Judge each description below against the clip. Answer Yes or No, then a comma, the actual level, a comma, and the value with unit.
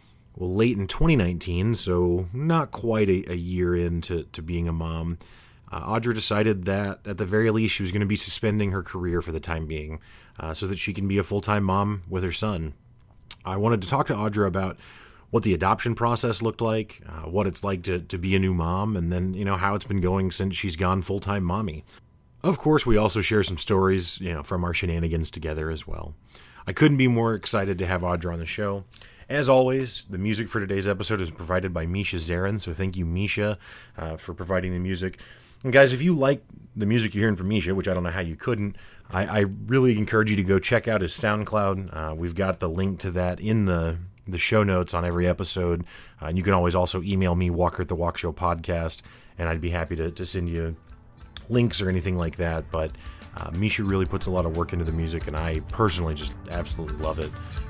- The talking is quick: Yes, fast, 230 wpm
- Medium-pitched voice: No, very low, 95 Hz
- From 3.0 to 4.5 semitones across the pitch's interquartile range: Yes, average, 3.5 semitones